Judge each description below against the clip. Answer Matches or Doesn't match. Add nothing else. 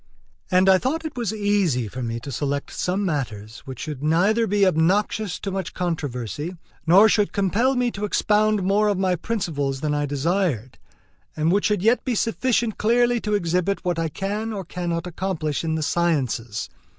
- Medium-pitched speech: Matches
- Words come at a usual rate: Matches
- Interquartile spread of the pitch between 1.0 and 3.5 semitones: Doesn't match